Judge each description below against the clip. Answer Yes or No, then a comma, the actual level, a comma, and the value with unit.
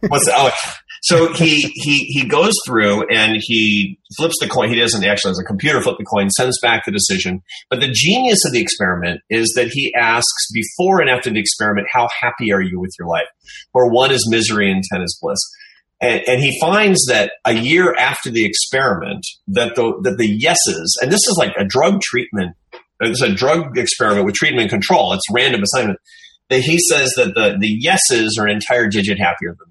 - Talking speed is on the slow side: No, fast, 205 wpm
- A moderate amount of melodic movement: No, wide, 7.6 semitones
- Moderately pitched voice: No, low, 120 Hz